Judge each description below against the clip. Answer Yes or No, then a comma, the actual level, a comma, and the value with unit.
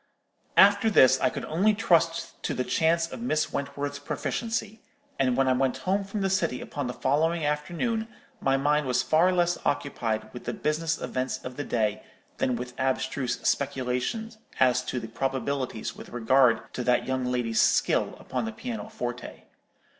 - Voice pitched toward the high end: No, medium, 140 Hz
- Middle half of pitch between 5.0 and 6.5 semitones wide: Yes, average, 5.3 semitones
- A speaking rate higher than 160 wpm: Yes, average, 170 wpm